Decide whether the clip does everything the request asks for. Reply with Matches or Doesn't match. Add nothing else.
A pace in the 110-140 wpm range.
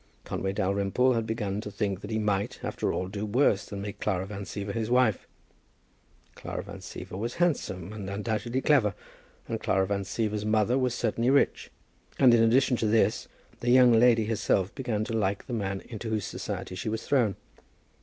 Doesn't match